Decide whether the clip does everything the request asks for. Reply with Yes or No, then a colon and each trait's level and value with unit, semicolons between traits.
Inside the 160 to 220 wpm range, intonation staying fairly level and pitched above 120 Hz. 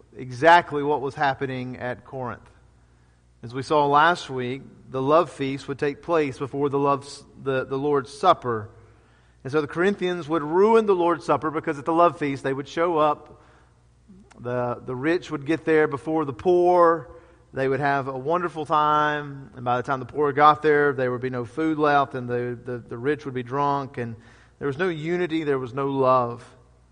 No: average, 195 wpm; average, 3.6 semitones; medium, 140 Hz